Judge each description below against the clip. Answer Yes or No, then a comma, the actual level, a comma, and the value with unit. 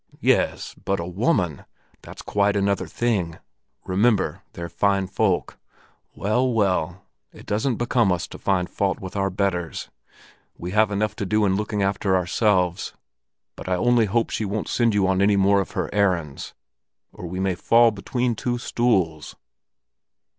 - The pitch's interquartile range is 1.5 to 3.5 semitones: Yes, average, 2.8 semitones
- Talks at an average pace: Yes, average, 160 wpm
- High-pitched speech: No, low, 100 Hz